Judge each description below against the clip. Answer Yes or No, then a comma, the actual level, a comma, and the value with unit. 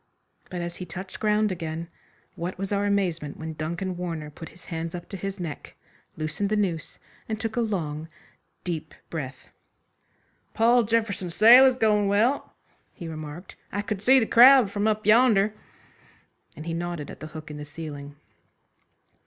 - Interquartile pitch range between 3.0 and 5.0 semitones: Yes, average, 4.7 semitones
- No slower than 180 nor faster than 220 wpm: No, average, 170 wpm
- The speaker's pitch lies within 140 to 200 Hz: Yes, medium, 185 Hz